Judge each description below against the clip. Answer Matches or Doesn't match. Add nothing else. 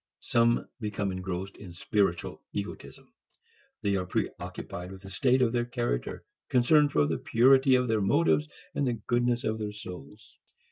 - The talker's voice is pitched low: Matches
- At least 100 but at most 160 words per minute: Matches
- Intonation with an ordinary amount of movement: Matches